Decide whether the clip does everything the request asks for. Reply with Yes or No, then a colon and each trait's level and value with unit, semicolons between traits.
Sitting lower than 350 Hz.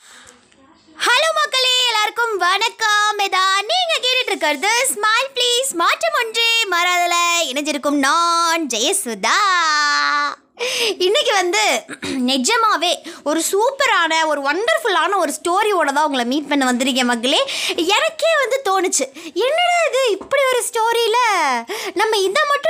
No: very high, 355 Hz